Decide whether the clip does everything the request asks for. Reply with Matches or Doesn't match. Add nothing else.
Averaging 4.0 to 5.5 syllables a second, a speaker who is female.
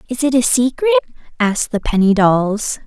Matches